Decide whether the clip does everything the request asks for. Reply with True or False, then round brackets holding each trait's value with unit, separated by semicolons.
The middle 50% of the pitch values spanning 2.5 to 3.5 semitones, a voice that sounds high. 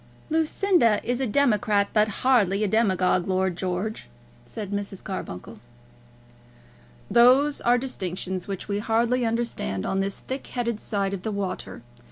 False (3.9 semitones; 210 Hz)